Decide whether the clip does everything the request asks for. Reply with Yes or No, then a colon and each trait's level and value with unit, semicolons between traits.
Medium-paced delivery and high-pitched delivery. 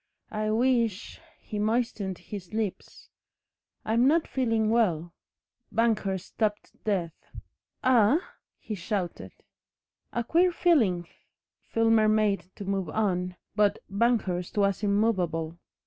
No: slow, 110 wpm; high, 215 Hz